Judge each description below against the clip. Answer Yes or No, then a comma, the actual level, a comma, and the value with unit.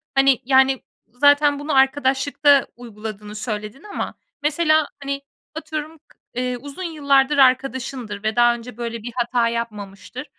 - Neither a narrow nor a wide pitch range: Yes, average, 3.6 semitones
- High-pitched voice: Yes, very high, 265 Hz